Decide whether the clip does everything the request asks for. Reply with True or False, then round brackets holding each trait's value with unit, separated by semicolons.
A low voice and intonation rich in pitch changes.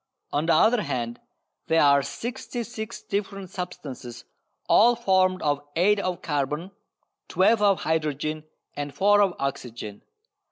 False (175 Hz; 6.0 semitones)